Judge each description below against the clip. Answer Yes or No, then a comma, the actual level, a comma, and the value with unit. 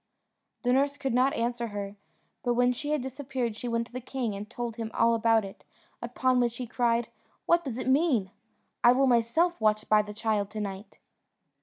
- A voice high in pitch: Yes, high, 240 Hz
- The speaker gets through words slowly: No, average, 200 wpm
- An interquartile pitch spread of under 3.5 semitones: Yes, average, 2.7 semitones